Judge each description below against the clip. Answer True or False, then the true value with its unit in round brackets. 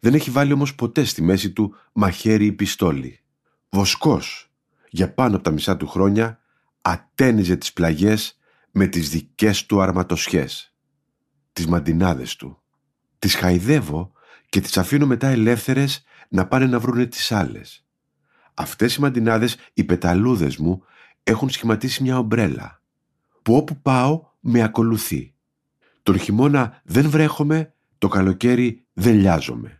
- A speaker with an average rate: True (135 wpm)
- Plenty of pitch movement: True (5.8 semitones)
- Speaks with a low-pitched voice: True (115 Hz)